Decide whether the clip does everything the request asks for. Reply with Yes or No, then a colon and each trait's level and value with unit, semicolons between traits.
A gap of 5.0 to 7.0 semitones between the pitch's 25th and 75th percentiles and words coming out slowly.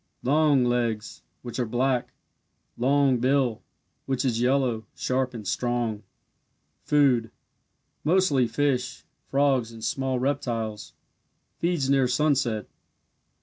No: narrow, 2.6 semitones; slow, 105 wpm